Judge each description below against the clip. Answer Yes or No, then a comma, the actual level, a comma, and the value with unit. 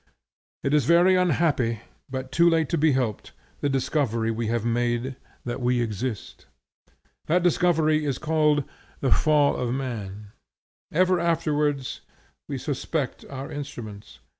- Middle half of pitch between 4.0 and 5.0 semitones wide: Yes, average, 4.7 semitones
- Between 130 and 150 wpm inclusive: Yes, slow, 135 wpm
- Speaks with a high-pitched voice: No, low, 135 Hz